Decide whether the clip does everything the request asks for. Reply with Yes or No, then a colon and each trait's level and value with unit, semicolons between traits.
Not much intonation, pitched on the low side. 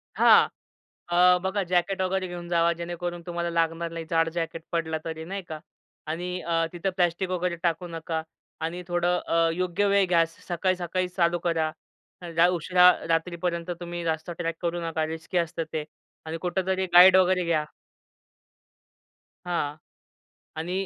No: narrow, 1.5 semitones; medium, 170 Hz